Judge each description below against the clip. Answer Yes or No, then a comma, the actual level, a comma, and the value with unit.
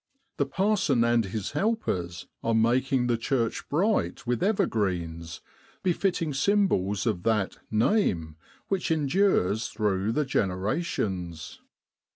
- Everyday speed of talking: No, slow, 120 wpm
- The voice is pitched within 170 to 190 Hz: No, low, 115 Hz